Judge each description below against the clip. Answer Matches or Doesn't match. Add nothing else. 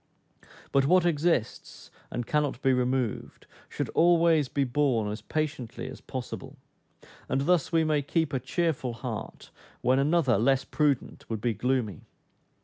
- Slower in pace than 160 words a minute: Matches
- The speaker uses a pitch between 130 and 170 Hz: Matches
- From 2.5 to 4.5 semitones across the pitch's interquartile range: Matches